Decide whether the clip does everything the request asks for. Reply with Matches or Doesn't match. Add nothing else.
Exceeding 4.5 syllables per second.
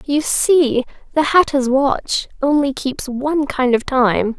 Doesn't match